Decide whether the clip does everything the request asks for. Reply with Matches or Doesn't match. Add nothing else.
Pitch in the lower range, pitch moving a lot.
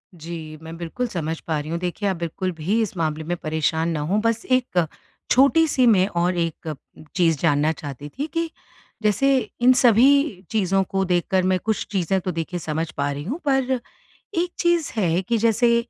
Doesn't match